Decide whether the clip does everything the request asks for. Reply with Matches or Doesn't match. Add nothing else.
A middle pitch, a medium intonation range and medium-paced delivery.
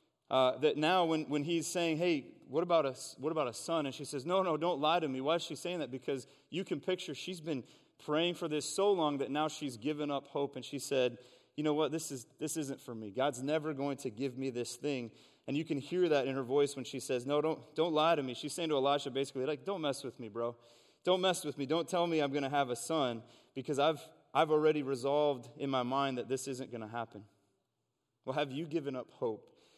Doesn't match